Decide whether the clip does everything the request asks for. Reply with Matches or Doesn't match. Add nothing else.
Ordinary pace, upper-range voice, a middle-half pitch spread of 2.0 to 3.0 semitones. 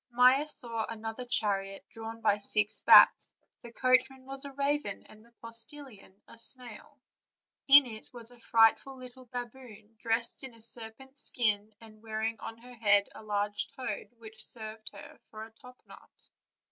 Matches